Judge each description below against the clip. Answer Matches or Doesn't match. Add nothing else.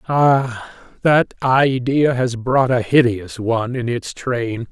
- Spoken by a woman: Doesn't match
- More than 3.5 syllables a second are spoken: Doesn't match